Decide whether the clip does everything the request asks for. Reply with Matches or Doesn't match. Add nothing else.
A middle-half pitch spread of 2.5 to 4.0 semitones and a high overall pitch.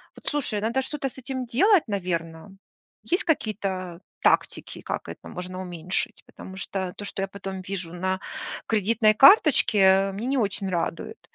Doesn't match